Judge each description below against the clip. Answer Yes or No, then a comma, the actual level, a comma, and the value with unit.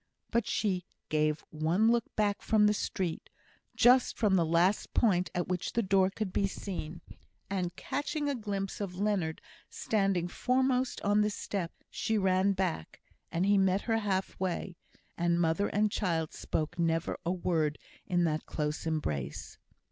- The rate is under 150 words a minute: No, average, 160 wpm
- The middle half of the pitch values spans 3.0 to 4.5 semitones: Yes, average, 3.6 semitones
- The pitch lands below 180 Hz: No, high, 190 Hz